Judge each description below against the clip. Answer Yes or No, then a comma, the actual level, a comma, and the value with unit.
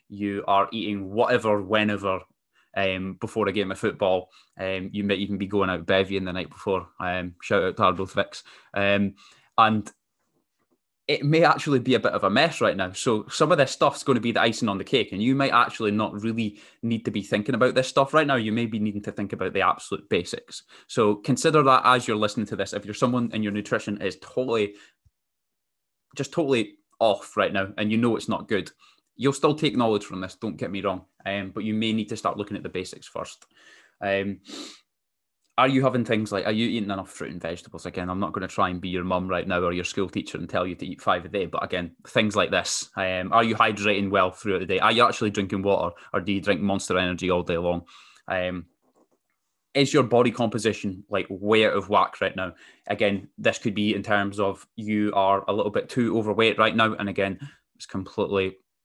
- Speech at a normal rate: No, fast, 225 wpm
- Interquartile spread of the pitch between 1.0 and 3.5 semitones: Yes, average, 3.0 semitones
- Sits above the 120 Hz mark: No, low, 105 Hz